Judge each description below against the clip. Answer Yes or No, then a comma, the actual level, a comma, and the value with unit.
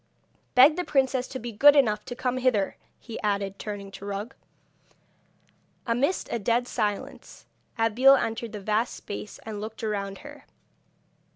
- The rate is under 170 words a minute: Yes, average, 150 wpm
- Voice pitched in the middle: No, high, 225 Hz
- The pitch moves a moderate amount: Yes, average, 3.7 semitones